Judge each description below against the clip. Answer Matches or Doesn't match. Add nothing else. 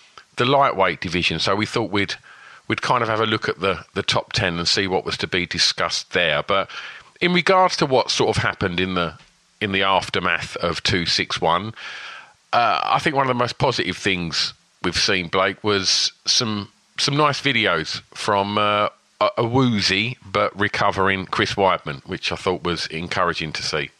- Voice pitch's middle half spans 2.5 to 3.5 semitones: Matches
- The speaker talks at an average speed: Matches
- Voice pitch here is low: Matches